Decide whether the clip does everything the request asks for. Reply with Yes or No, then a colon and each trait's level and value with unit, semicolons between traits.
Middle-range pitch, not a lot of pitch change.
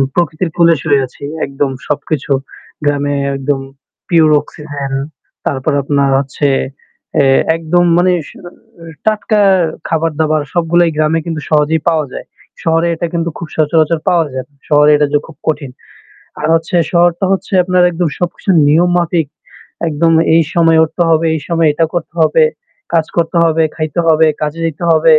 Yes: medium, 160 Hz; narrow, 2.3 semitones